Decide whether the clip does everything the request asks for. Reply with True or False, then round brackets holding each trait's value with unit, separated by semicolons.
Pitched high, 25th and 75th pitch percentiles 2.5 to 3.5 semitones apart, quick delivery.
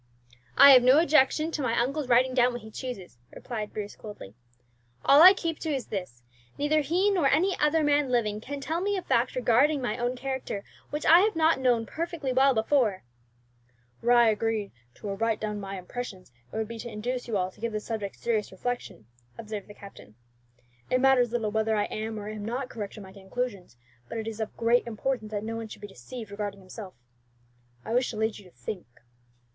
False (235 Hz; 4.1 semitones; 215 wpm)